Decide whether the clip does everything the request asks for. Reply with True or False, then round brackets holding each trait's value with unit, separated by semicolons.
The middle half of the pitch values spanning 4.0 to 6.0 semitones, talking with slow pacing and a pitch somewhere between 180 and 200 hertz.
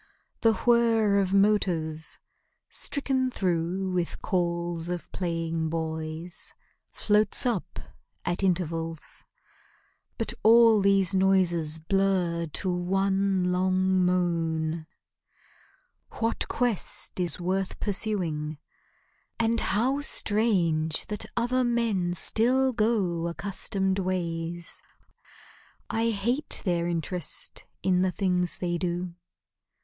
False (3.6 semitones; 95 wpm; 185 Hz)